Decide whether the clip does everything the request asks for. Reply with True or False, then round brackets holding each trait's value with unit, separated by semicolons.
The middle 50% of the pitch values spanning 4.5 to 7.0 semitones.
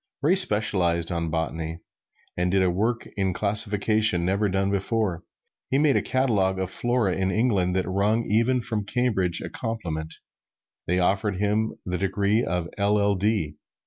False (3.4 semitones)